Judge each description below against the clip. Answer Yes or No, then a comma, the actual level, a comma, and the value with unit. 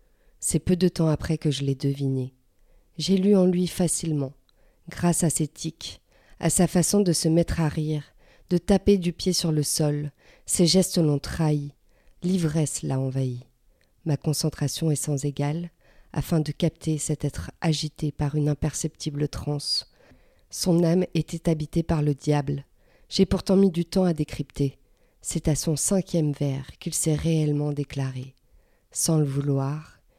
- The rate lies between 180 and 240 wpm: No, average, 160 wpm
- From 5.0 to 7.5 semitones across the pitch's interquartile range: No, average, 2.9 semitones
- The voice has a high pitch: No, medium, 155 Hz